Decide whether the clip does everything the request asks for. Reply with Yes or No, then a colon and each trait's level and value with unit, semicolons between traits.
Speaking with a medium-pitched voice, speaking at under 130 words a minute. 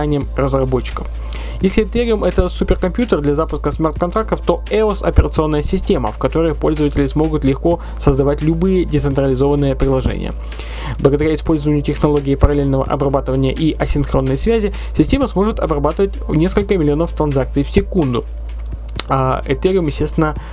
Yes: medium, 150 Hz; average, 115 wpm